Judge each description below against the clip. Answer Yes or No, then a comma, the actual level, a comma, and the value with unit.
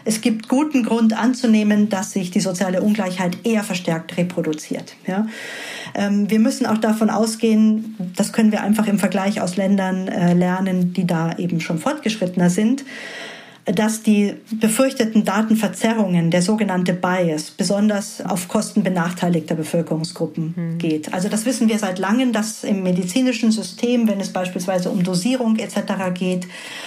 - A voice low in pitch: No, high, 205 Hz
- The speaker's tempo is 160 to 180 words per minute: No, average, 145 wpm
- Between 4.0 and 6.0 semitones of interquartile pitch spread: No, average, 3.4 semitones